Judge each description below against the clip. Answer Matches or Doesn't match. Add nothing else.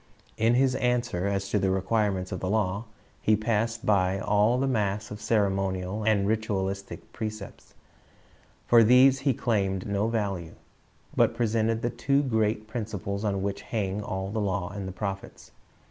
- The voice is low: Matches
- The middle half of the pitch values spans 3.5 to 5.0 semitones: Doesn't match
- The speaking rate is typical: Matches